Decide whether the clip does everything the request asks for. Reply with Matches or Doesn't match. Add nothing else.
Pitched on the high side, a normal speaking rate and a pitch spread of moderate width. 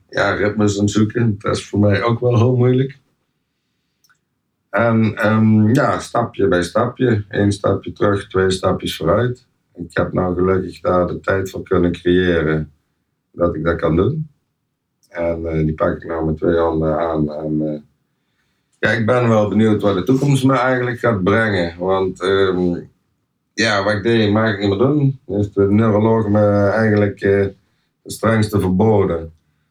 Doesn't match